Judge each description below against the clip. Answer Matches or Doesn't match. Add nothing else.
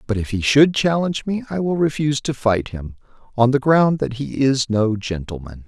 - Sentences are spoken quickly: Matches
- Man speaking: Matches